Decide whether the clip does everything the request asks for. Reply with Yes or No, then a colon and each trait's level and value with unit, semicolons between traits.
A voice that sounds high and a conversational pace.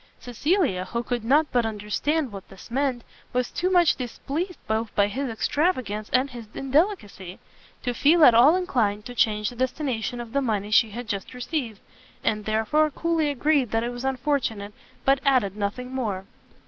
Yes: high, 245 Hz; average, 175 wpm